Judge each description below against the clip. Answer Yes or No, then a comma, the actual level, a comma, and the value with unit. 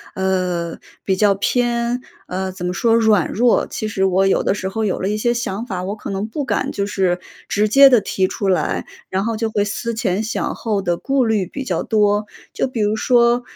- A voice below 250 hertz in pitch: Yes, high, 210 Hz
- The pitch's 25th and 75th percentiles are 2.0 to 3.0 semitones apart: No, average, 3.6 semitones